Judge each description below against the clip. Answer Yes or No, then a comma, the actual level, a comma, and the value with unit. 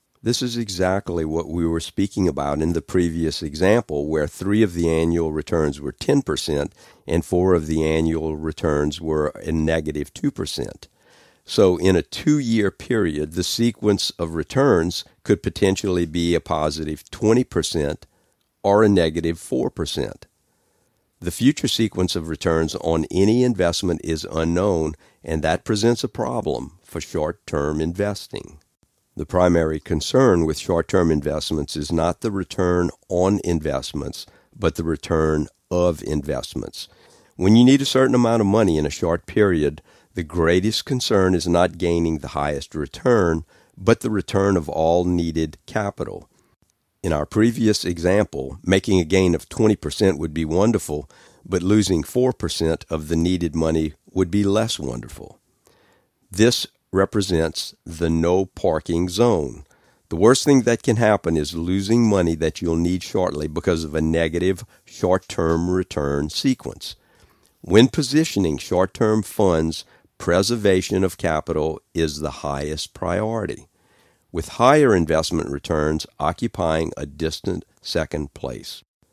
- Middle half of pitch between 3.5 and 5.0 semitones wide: Yes, average, 3.8 semitones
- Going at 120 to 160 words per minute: Yes, average, 140 wpm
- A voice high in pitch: No, very low, 85 Hz